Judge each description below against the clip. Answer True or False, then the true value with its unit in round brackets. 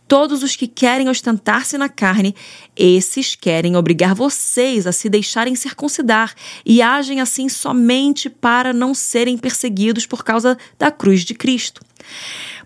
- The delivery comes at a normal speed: True (140 wpm)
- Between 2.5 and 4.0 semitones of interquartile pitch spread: True (3.6 semitones)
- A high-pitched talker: True (245 Hz)